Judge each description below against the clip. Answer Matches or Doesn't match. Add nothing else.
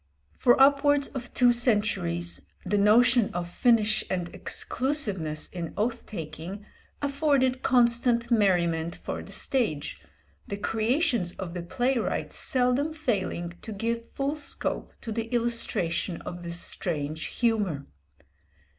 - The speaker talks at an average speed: Doesn't match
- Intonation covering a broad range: Matches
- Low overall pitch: Doesn't match